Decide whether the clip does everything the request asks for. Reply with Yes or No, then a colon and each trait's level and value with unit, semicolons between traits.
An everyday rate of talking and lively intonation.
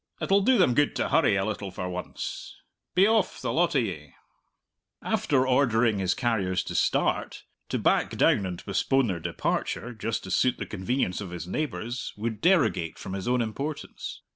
Yes: average, 180 wpm; wide, 6.5 semitones